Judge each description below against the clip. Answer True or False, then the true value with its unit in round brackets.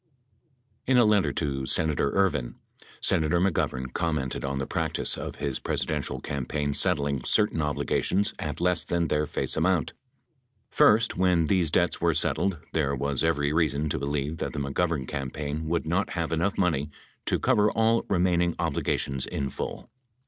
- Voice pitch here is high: False (80 Hz)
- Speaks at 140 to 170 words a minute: True (160 wpm)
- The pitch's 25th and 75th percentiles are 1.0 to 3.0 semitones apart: False (4.0 semitones)